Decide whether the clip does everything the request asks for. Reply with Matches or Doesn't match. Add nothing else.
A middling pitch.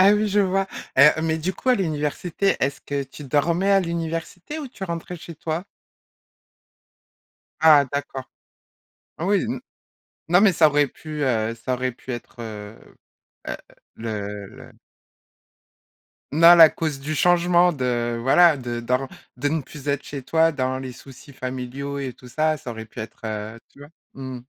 Matches